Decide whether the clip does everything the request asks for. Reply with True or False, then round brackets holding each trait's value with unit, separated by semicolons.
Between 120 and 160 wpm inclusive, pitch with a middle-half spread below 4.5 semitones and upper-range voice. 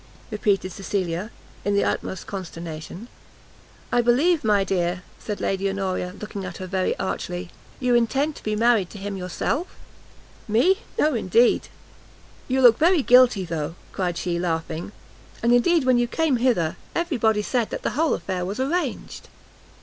False (155 wpm; 5.2 semitones; 210 Hz)